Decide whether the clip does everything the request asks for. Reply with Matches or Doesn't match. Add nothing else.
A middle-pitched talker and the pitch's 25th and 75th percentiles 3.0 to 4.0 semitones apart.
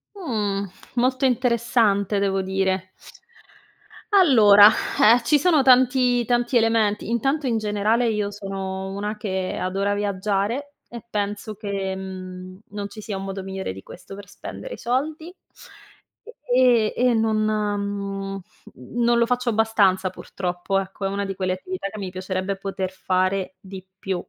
Doesn't match